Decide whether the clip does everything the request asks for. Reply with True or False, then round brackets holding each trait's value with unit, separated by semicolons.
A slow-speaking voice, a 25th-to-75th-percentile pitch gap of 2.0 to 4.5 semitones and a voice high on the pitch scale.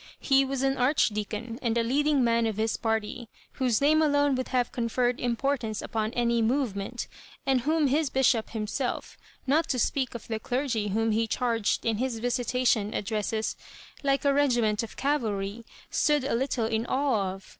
False (175 wpm; 3.5 semitones; 240 Hz)